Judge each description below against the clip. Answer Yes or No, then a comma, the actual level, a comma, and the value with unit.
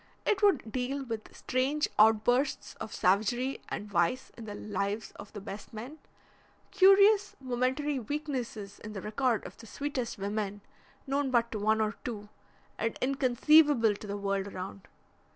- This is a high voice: Yes, high, 235 Hz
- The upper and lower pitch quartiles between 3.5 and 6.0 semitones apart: Yes, average, 4.7 semitones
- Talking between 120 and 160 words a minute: Yes, average, 150 wpm